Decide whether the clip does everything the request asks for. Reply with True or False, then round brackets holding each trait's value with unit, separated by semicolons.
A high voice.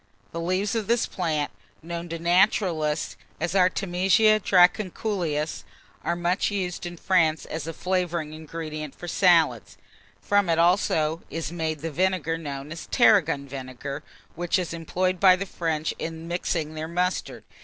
False (170 Hz)